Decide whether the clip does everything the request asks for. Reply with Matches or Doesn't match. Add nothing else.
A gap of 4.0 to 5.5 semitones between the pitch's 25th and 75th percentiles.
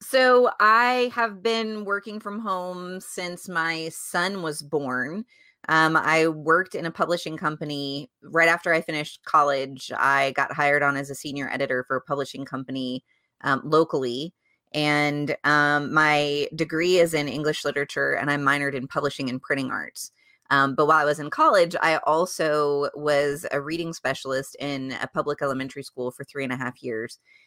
Doesn't match